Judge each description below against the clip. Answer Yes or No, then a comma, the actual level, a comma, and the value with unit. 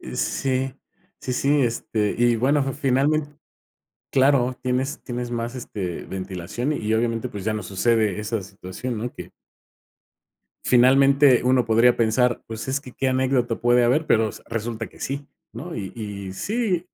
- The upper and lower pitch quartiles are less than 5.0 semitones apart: Yes, average, 3.3 semitones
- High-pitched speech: No, low, 120 Hz